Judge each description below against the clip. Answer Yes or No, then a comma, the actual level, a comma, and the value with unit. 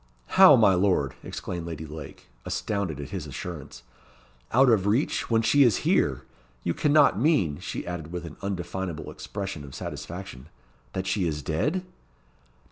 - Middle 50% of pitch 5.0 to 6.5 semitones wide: Yes, average, 5.3 semitones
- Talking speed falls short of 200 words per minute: Yes, average, 150 wpm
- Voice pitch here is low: Yes, very low, 90 Hz